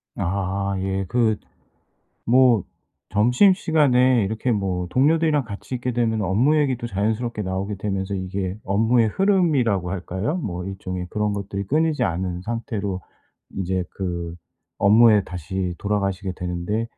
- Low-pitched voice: Yes, low, 100 Hz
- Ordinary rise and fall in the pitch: Yes, average, 4.4 semitones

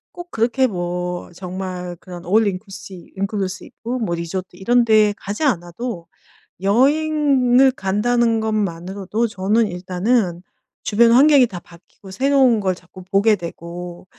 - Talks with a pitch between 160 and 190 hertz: No, high, 200 Hz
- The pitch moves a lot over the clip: No, average, 4.7 semitones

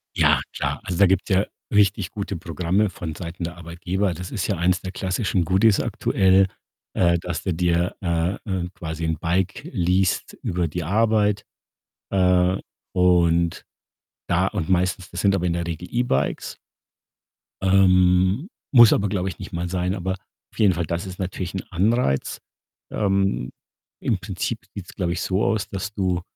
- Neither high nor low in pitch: No, very low, 90 Hz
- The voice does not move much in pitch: Yes, narrow, 2.1 semitones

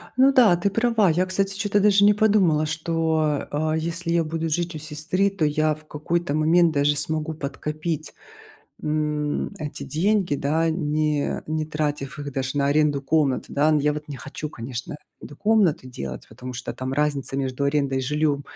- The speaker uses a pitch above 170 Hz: No, medium, 155 Hz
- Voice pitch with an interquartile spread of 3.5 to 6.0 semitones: No, average, 2.8 semitones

